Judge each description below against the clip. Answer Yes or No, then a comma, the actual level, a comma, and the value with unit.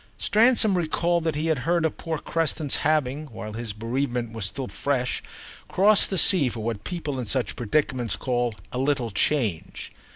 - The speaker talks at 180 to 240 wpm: No, average, 170 wpm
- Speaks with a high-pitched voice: No, low, 135 Hz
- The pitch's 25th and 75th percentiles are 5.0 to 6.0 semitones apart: Yes, wide, 5.5 semitones